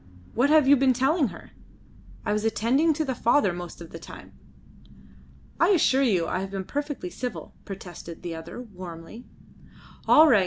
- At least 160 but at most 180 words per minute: Yes, average, 170 wpm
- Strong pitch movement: Yes, wide, 7.3 semitones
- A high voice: Yes, high, 225 Hz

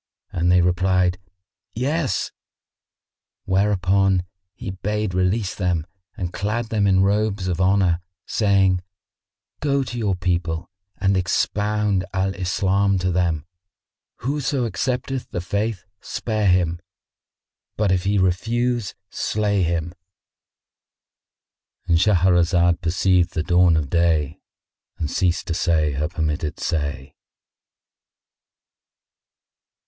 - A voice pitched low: Yes, very low, 95 Hz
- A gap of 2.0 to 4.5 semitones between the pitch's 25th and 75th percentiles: Yes, average, 3.0 semitones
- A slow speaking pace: Yes, slow, 105 wpm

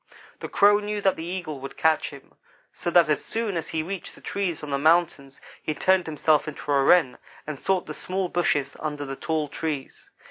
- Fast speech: Yes, fast, 210 wpm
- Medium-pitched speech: Yes, medium, 160 Hz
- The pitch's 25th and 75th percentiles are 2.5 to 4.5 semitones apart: Yes, average, 3.8 semitones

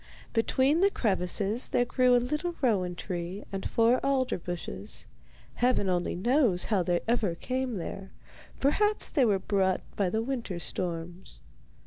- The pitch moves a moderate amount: No, wide, 5.8 semitones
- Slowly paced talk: No, average, 145 wpm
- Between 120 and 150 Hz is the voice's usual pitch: No, high, 215 Hz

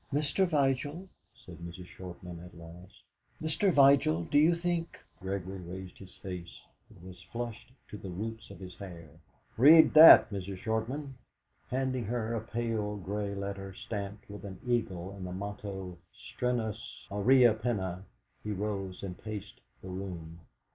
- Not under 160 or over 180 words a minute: No, average, 150 wpm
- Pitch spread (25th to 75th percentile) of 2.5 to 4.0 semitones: No, average, 4.7 semitones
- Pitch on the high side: No, low, 100 Hz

